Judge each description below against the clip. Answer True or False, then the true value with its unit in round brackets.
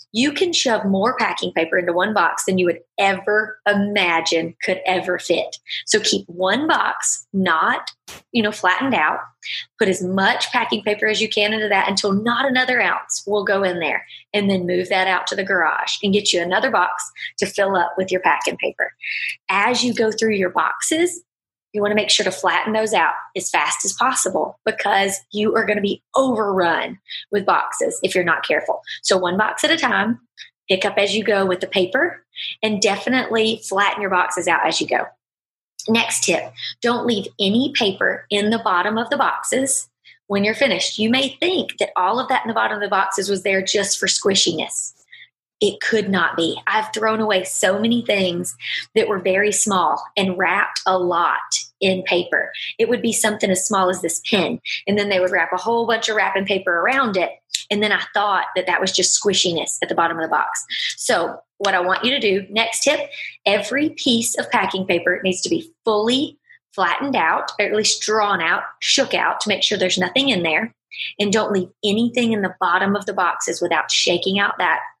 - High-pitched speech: True (205 Hz)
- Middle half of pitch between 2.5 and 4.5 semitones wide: True (3.3 semitones)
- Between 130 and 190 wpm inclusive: False (205 wpm)